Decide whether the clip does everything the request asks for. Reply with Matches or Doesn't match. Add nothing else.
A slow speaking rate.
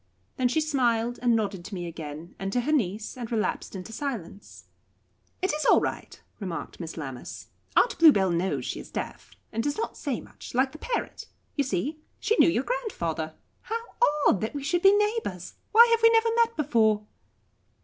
Doesn't match